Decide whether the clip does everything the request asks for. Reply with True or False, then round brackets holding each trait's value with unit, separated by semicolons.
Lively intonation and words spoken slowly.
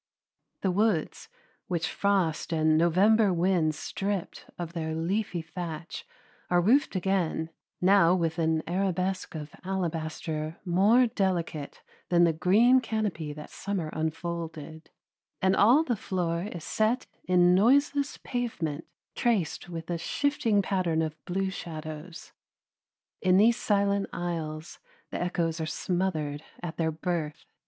False (3.5 semitones; 125 wpm)